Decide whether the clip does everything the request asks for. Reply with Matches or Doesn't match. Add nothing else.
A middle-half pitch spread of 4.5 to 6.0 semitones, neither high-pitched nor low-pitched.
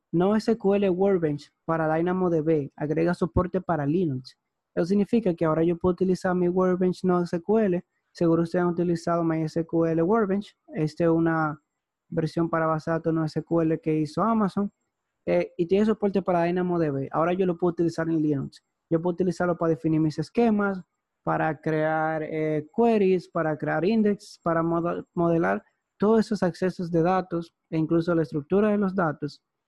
Doesn't match